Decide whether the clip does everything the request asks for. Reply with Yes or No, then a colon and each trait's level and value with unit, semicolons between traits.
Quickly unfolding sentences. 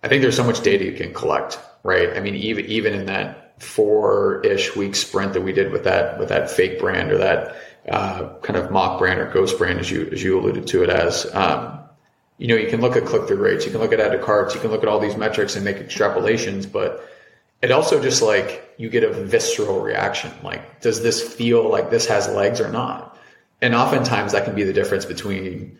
Yes: fast, 235 wpm